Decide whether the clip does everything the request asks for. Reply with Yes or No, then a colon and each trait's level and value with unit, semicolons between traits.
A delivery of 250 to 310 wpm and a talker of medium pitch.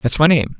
Yes: fast, 305 wpm; medium, 145 Hz